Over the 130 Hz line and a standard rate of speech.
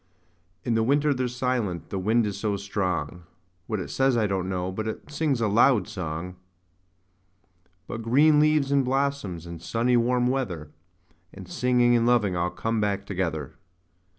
No: low, 110 Hz; average, 170 wpm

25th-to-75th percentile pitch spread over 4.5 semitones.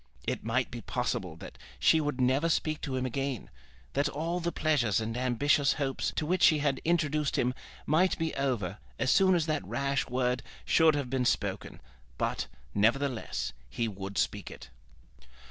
No: average, 3.9 semitones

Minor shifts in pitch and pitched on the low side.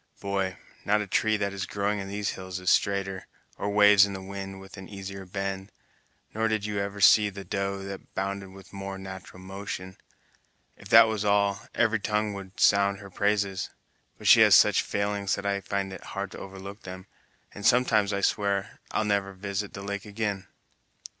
Yes: narrow, 0.9 semitones; low, 100 Hz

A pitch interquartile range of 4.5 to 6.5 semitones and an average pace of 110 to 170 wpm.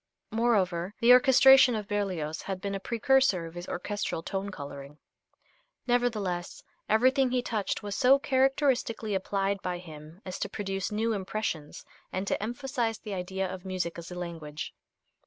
Yes: average, 4.8 semitones; average, 155 wpm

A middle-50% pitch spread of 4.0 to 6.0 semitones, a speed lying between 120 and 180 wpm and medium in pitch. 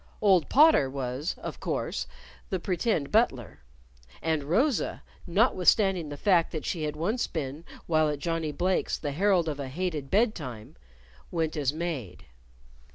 Yes: average, 4.5 semitones; average, 150 wpm; medium, 160 Hz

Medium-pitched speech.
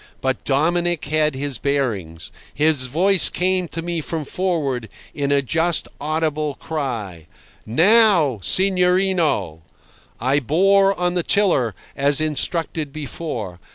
Yes: medium, 155 Hz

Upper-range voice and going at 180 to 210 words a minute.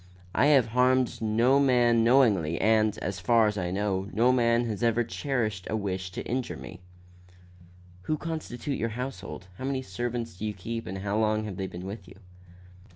No: low, 115 Hz; average, 185 wpm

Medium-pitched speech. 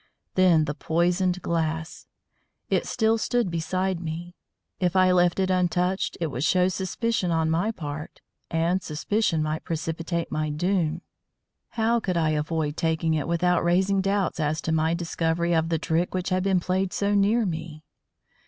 Yes: medium, 170 Hz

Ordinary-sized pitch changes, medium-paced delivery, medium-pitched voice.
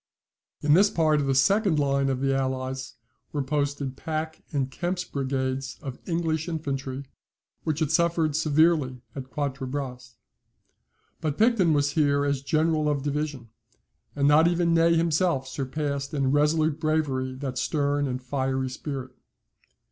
Yes: average, 3.0 semitones; average, 145 wpm; medium, 145 Hz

